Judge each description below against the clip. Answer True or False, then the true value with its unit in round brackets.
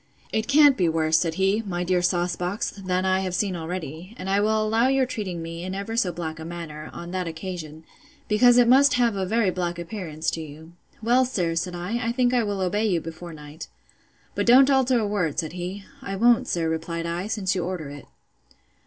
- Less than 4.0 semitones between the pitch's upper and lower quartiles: False (4.5 semitones)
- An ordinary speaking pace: False (215 wpm)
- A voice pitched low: False (185 Hz)